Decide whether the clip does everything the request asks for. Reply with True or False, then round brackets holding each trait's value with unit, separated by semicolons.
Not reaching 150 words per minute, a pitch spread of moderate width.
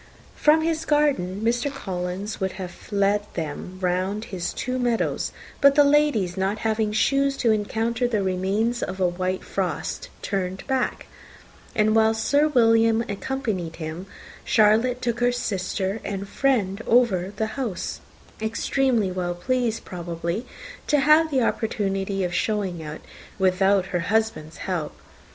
True (140 wpm; 4.6 semitones)